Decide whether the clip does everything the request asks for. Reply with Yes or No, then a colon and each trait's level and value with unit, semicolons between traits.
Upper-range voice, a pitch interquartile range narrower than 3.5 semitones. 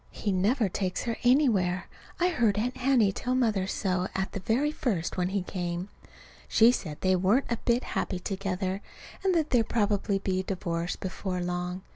No: high, 195 Hz; average, 4.5 semitones